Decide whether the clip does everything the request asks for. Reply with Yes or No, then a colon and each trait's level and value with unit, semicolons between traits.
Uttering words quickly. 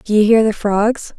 Yes: fast, 255 wpm